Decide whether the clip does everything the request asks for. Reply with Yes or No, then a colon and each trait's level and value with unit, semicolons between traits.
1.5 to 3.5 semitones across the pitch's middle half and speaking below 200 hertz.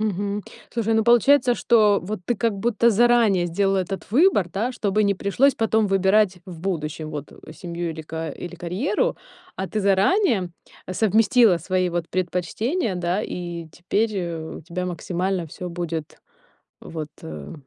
No: average, 4.1 semitones; high, 190 Hz